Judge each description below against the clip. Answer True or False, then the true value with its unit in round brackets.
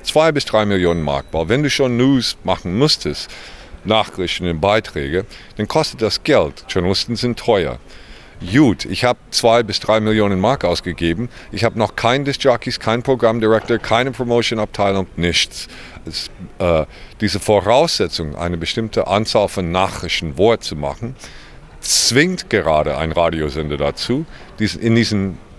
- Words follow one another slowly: False (140 wpm)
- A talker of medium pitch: False (105 Hz)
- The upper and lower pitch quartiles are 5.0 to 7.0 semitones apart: True (5.4 semitones)